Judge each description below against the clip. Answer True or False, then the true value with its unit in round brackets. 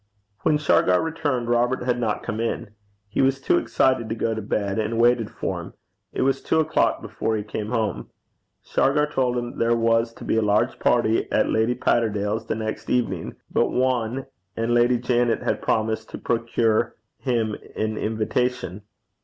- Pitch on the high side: False (115 Hz)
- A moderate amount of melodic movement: False (2.1 semitones)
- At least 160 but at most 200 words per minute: True (175 wpm)